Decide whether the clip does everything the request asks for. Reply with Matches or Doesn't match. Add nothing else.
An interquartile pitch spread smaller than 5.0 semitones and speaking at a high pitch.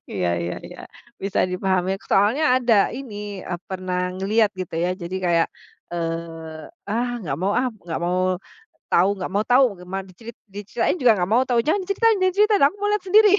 Doesn't match